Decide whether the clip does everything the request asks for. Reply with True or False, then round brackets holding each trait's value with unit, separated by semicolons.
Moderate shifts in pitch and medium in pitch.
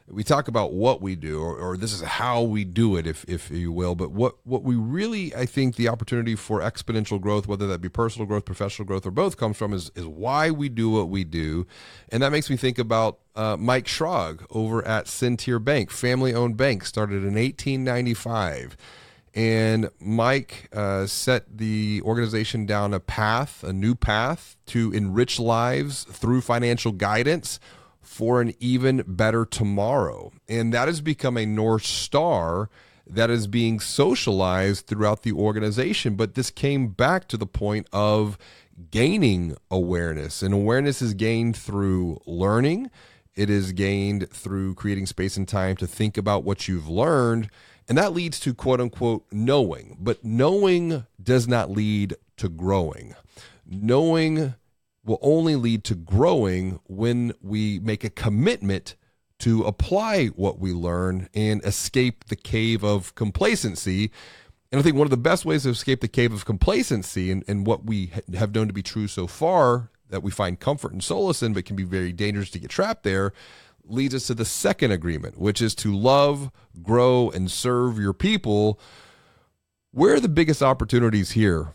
False (3.9 semitones; 110 Hz)